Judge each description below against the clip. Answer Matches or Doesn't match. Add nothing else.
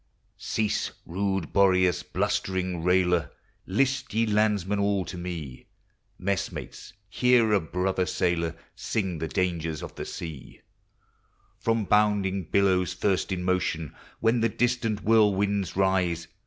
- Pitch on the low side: Matches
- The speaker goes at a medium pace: Doesn't match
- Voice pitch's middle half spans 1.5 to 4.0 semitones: Matches